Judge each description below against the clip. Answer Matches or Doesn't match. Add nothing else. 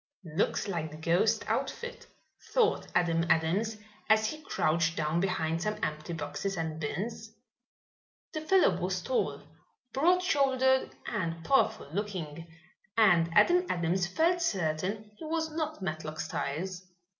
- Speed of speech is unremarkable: Doesn't match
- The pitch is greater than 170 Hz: Matches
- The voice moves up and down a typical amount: Doesn't match